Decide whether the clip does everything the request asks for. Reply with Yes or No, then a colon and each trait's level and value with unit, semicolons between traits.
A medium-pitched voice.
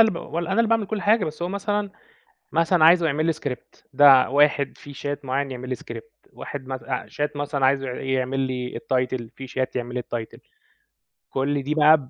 Yes: medium, 145 Hz